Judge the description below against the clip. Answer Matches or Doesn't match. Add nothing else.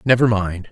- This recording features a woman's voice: Doesn't match